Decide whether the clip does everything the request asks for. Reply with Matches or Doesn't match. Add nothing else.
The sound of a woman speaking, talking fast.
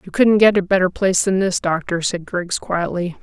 Matches